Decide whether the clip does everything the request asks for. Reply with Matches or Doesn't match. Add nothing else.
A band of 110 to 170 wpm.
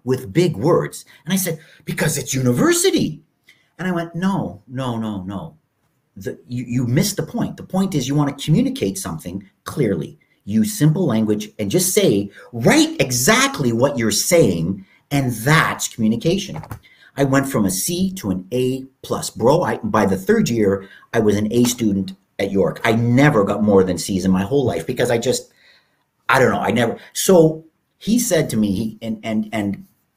Doesn't match